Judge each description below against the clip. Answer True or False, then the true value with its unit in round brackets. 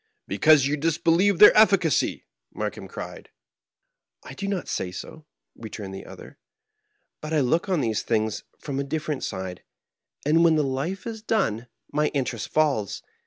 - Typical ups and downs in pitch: False (6.0 semitones)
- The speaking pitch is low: False (150 Hz)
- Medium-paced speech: True (160 wpm)